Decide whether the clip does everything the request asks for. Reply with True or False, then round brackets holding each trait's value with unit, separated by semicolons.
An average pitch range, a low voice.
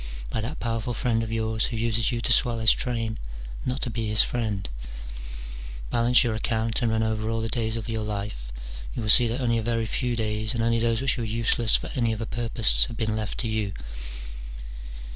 False (1.2 semitones; 115 Hz)